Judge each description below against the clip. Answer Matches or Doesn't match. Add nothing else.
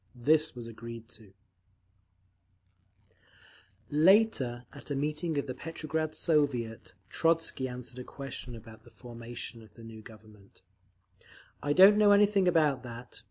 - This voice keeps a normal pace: Doesn't match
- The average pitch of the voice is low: Matches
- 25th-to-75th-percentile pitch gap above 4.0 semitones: Matches